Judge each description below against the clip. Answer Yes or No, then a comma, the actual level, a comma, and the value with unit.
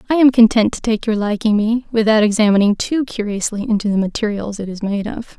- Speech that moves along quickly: Yes, fast, 210 wpm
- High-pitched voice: Yes, high, 215 Hz